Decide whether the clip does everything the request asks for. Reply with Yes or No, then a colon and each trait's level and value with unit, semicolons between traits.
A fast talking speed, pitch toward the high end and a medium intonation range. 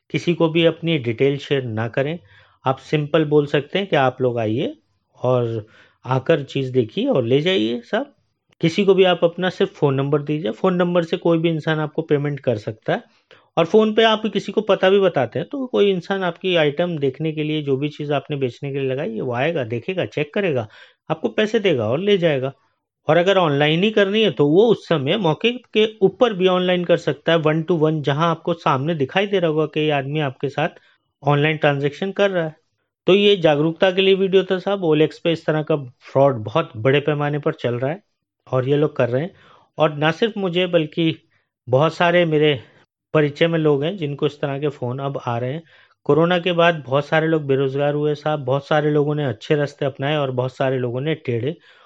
No: fast, 215 wpm; medium, 155 Hz; average, 4.1 semitones